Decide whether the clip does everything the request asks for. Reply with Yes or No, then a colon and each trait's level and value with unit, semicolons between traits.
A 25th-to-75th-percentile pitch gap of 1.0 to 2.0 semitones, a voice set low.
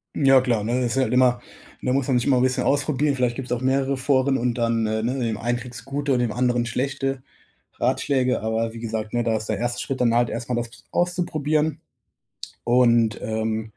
No: narrow, 2.5 semitones; low, 125 Hz